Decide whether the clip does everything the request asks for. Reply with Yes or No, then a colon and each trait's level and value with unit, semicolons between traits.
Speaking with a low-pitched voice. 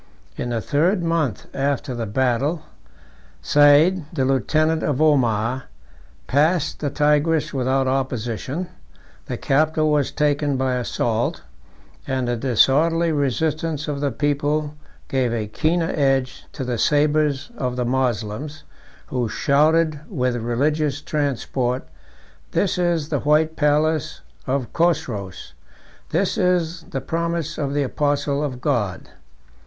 No: medium, 145 Hz